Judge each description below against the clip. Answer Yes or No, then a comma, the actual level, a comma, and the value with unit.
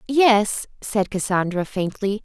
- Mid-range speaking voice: No, high, 210 Hz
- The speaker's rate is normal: No, slow, 105 wpm